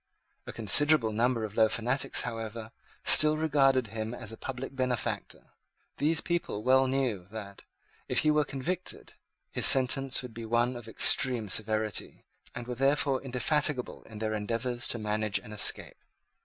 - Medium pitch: No, low, 120 Hz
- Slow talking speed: No, average, 155 wpm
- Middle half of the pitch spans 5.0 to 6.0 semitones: No, average, 3.6 semitones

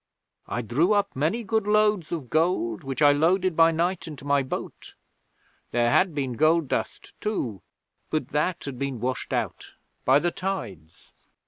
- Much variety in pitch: Yes, wide, 5.8 semitones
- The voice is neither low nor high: Yes, medium, 155 Hz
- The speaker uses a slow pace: No, average, 160 wpm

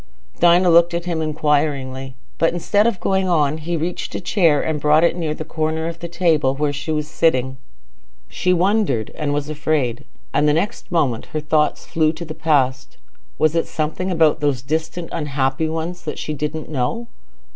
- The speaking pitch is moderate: Yes, medium, 155 Hz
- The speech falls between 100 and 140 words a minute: No, average, 180 wpm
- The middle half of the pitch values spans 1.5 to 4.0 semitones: Yes, narrow, 2.5 semitones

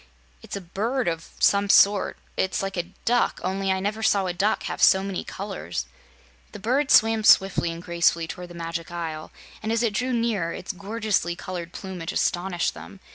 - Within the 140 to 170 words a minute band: No, average, 185 wpm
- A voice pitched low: No, high, 190 Hz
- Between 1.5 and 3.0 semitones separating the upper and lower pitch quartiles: No, average, 3.7 semitones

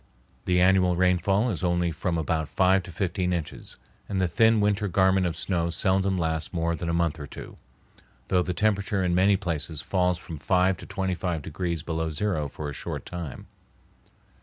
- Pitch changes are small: Yes, narrow, 2.3 semitones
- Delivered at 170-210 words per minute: Yes, average, 185 wpm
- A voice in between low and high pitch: No, very low, 90 Hz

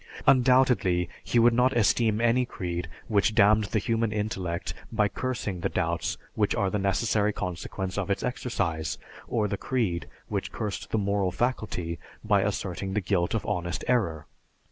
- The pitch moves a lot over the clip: No, average, 4.1 semitones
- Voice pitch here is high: No, low, 105 Hz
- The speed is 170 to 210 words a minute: No, average, 160 wpm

